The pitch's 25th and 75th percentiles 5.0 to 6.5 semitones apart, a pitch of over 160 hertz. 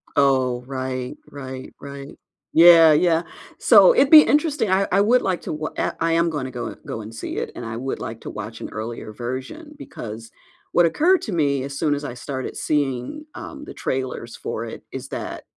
No: wide, 5.6 semitones; medium, 140 Hz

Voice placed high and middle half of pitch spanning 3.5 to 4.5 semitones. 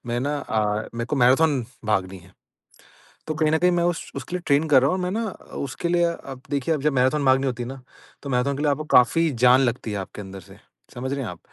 No: low, 135 Hz; average, 3.8 semitones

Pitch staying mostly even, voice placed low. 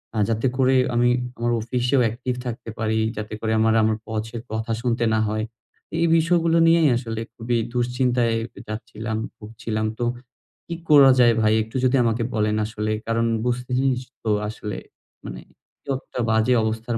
Yes: narrow, 2.2 semitones; low, 115 Hz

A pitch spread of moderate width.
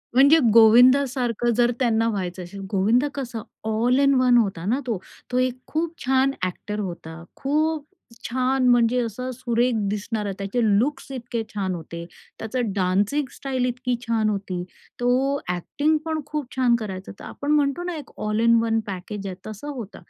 Yes: average, 4.1 semitones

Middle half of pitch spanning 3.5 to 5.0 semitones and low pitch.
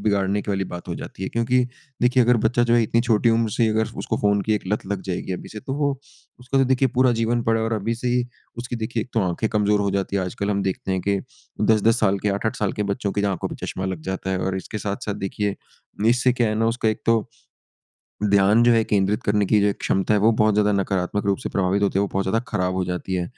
No: average, 2.8 semitones; low, 105 Hz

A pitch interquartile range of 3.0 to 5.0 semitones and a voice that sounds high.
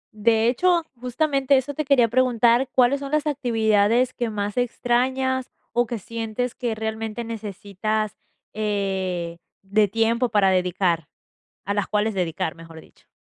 Yes: average, 3.6 semitones; high, 225 Hz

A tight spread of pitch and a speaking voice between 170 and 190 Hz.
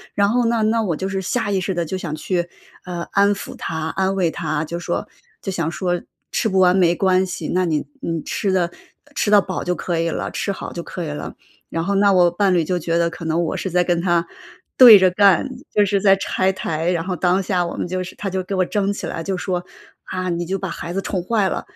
Yes: narrow, 2.2 semitones; medium, 185 Hz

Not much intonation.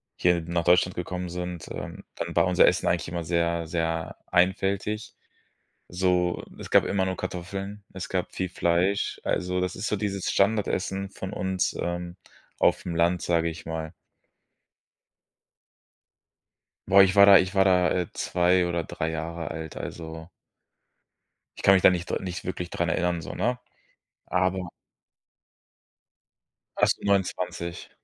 Yes: narrow, 1.9 semitones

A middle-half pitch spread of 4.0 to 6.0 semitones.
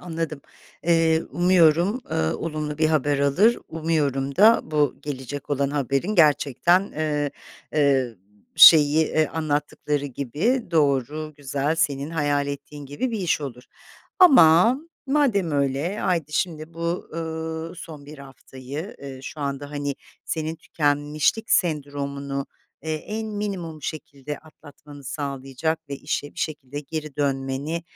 No: average, 2.7 semitones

